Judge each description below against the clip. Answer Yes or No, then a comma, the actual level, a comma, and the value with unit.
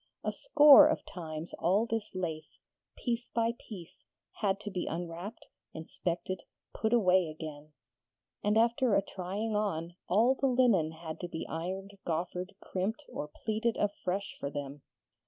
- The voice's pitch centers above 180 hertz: Yes, high, 190 Hz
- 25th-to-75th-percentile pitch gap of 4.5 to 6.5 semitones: Yes, average, 4.9 semitones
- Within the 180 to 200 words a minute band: No, average, 145 wpm